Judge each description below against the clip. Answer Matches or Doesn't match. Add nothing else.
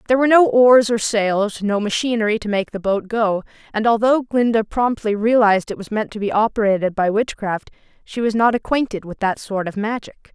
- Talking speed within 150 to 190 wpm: Doesn't match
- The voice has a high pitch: Matches